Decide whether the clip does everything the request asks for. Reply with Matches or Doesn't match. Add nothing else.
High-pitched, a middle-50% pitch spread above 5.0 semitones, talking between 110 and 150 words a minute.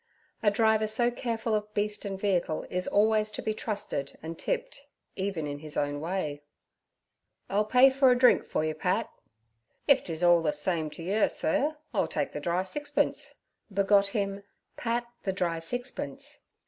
Doesn't match